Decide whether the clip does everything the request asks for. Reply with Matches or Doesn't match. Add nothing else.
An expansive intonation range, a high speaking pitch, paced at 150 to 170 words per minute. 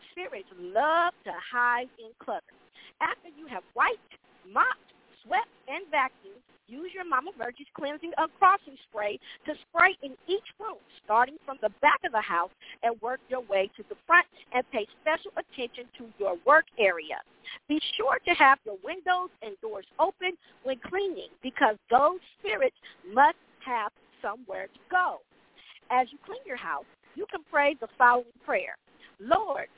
Matches